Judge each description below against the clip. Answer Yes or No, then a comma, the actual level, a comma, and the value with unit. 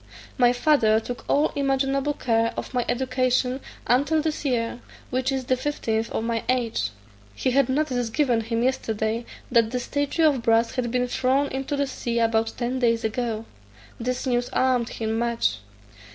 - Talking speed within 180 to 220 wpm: No, average, 165 wpm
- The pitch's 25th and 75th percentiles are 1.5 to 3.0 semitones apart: Yes, narrow, 2.6 semitones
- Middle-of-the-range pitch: No, high, 245 Hz